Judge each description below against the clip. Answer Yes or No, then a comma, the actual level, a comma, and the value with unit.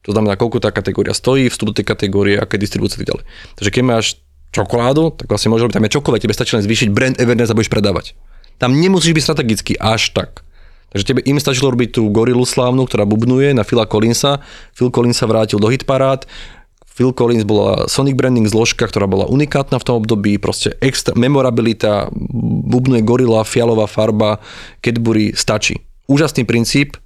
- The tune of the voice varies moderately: Yes, average, 3.3 semitones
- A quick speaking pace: Yes, fast, 180 wpm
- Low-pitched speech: Yes, low, 115 Hz